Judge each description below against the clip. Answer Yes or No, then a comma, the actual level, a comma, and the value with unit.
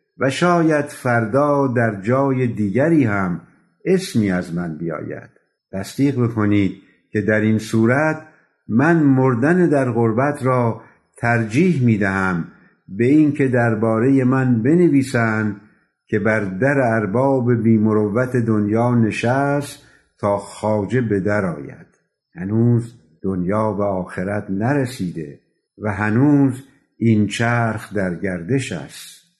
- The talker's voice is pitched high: No, low, 115 Hz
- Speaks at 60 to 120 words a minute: Yes, average, 110 wpm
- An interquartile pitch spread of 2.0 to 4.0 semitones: No, average, 4.5 semitones